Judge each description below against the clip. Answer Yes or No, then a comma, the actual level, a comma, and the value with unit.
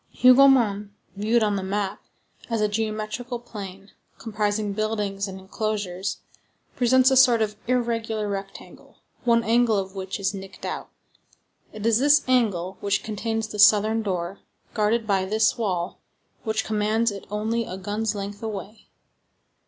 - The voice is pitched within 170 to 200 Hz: No, high, 215 Hz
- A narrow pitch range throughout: Yes, narrow, 2.3 semitones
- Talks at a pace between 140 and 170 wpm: Yes, average, 145 wpm